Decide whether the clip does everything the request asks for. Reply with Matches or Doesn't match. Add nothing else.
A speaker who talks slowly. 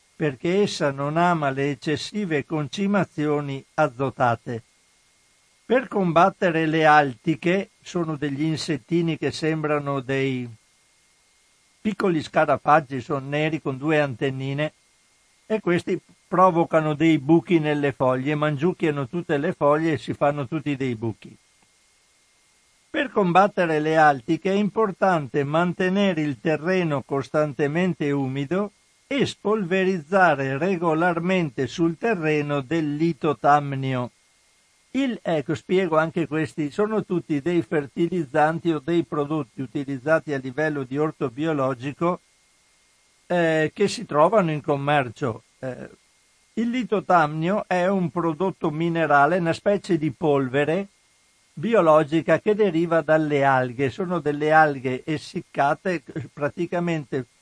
Matches